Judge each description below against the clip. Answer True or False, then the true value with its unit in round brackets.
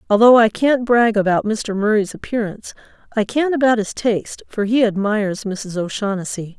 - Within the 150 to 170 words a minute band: True (165 wpm)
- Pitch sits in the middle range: False (215 Hz)